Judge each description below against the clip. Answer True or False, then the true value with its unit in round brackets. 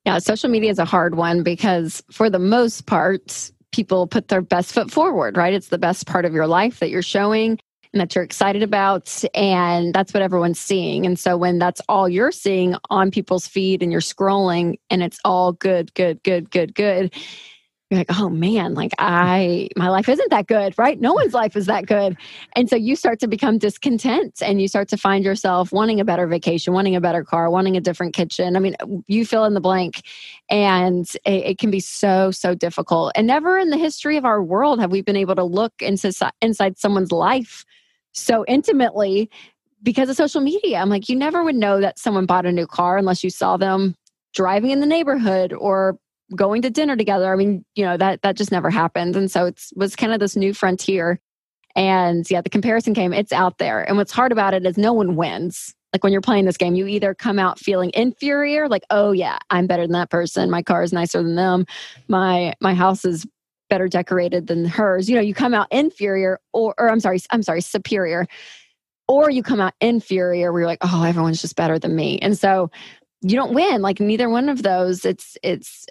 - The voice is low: False (195 Hz)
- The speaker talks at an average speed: False (215 wpm)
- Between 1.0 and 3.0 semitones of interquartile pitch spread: False (3.4 semitones)